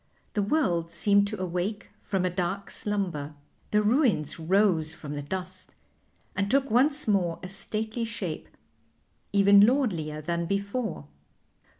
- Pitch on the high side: Yes, high, 195 Hz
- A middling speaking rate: No, slow, 130 wpm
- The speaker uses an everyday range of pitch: Yes, average, 3.7 semitones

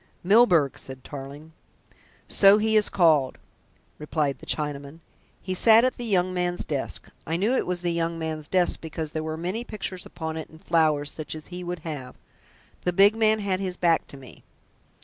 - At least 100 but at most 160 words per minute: No, average, 190 wpm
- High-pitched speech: No, medium, 170 Hz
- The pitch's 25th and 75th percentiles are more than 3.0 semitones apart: Yes, average, 3.5 semitones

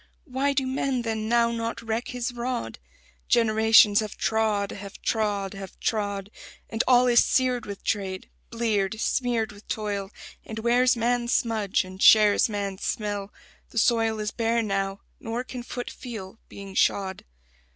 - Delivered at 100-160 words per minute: Yes, average, 150 wpm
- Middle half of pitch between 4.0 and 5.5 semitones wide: No, average, 2.8 semitones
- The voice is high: Yes, high, 220 Hz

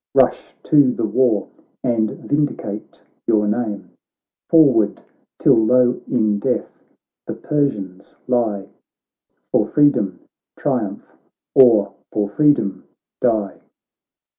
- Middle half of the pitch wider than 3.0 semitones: Yes, average, 3.8 semitones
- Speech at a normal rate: No, slow, 85 wpm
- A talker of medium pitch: No, low, 110 Hz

